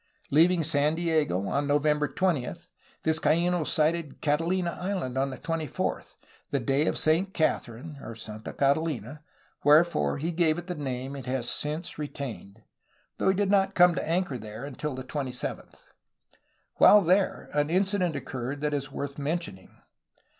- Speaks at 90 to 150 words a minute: Yes, average, 145 wpm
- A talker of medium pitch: Yes, medium, 150 Hz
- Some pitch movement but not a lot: Yes, average, 4.1 semitones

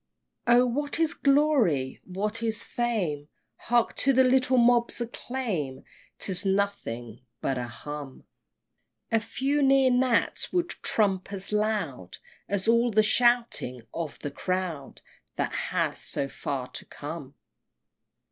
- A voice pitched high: Yes, high, 215 Hz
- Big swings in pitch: Yes, wide, 8.4 semitones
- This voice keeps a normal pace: No, slow, 130 wpm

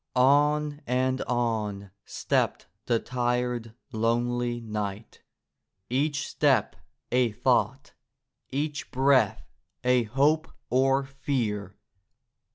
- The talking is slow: Yes, slow, 85 wpm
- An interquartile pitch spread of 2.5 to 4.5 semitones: Yes, average, 3.2 semitones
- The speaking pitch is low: Yes, low, 125 Hz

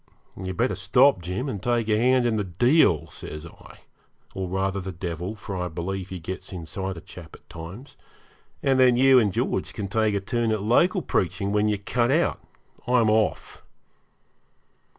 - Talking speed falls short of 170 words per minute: No, average, 180 wpm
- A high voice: No, low, 100 Hz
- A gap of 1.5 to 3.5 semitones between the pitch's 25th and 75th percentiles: No, average, 4.7 semitones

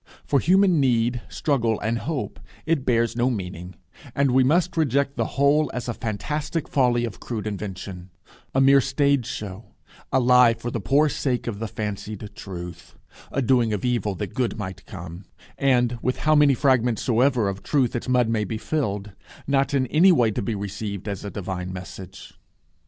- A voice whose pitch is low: Yes, low, 120 Hz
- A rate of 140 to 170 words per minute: No, average, 180 wpm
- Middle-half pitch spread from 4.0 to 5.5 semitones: Yes, average, 4.9 semitones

